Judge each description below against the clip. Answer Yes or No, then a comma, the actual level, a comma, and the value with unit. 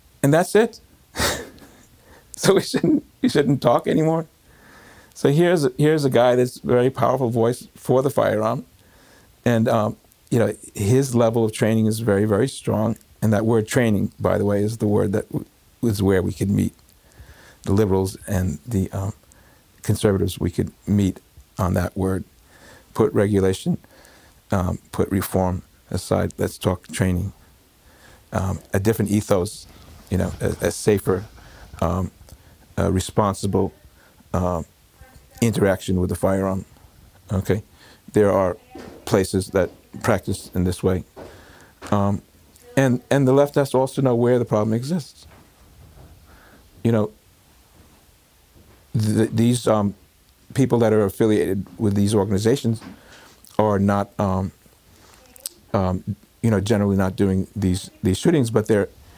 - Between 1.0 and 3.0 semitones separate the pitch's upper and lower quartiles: No, average, 3.5 semitones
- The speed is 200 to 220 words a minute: No, average, 140 wpm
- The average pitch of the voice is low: Yes, low, 100 Hz